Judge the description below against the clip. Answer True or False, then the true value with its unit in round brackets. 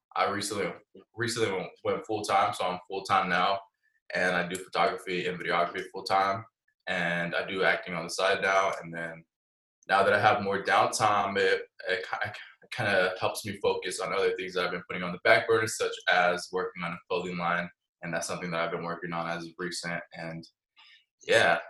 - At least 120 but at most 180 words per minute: False (205 wpm)